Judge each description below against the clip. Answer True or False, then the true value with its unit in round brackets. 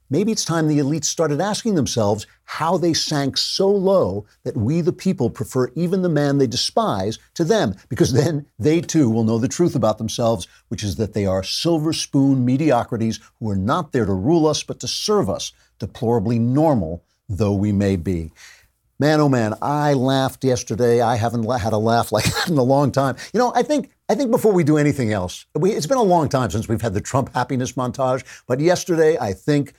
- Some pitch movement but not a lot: False (6.1 semitones)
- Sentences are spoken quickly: True (210 wpm)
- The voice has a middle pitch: False (130 Hz)